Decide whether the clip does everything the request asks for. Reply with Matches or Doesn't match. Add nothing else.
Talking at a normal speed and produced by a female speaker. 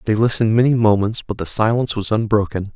Doesn't match